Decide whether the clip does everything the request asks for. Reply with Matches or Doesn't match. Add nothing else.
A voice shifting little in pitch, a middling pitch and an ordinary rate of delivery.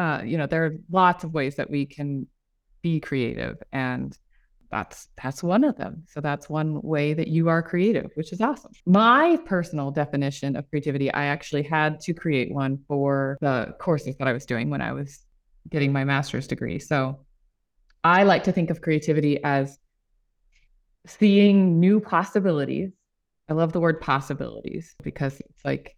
Doesn't match